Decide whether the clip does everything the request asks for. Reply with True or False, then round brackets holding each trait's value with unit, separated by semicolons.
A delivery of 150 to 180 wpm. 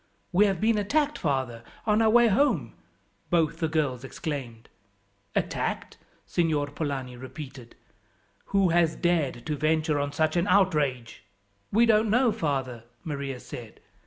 False (135 wpm)